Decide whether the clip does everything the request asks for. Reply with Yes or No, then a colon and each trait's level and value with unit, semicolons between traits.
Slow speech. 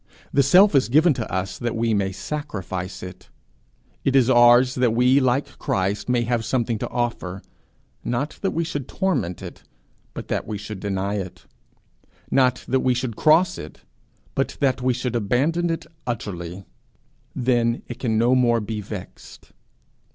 No: average, 165 wpm